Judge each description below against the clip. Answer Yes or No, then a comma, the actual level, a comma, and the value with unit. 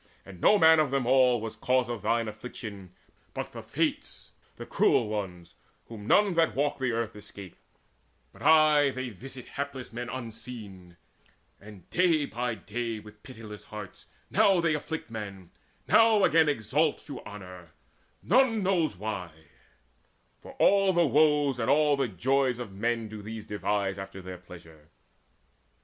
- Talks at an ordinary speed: Yes, average, 155 wpm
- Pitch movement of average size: No, wide, 5.9 semitones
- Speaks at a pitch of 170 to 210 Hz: No, low, 120 Hz